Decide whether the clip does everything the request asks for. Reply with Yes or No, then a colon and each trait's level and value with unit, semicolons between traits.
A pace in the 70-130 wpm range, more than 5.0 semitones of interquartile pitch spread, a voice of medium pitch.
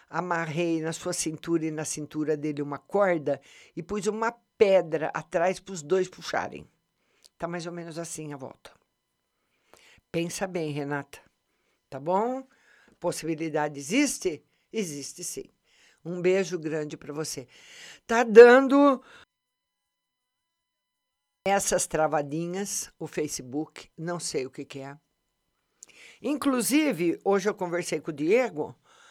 No: slow, 120 wpm; average, 4.6 semitones; medium, 170 Hz